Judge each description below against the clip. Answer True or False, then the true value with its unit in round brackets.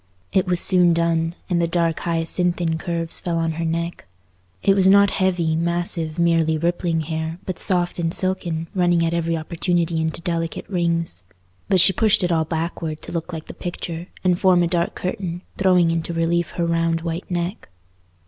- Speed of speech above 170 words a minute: True (180 wpm)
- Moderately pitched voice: True (170 Hz)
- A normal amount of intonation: False (1.3 semitones)